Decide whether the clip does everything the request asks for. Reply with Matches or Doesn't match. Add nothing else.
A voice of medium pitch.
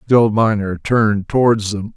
Doesn't match